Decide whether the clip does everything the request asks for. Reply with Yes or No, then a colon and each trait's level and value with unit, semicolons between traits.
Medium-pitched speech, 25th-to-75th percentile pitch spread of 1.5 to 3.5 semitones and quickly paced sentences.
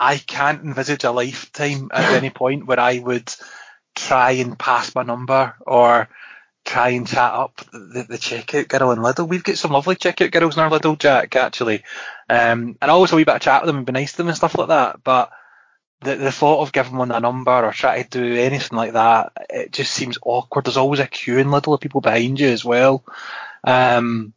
No: low, 130 Hz; average, 3.0 semitones; fast, 220 wpm